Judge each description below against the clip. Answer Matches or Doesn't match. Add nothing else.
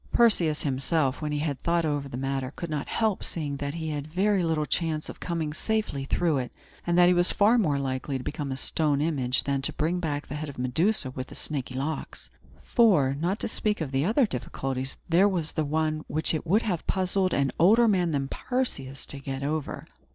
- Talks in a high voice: Doesn't match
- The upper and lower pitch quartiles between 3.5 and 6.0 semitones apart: Matches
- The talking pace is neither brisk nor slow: Doesn't match